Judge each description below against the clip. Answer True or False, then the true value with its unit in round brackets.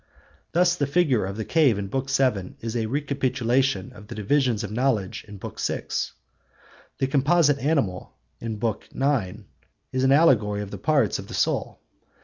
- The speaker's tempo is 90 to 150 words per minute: False (170 wpm)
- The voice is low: True (130 Hz)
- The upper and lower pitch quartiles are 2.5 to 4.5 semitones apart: False (5.1 semitones)